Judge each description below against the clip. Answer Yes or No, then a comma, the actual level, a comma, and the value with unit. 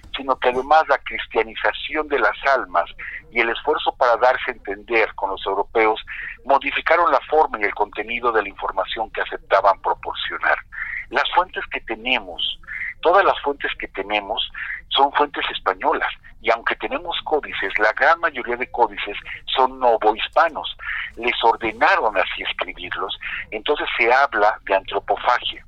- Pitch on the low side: Yes, low, 125 Hz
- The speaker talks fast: No, average, 145 wpm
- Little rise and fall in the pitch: No, average, 4.2 semitones